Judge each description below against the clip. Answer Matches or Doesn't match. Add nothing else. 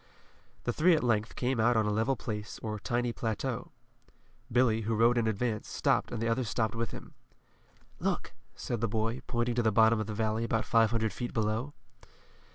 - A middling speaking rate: Matches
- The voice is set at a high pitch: Doesn't match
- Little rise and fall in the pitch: Matches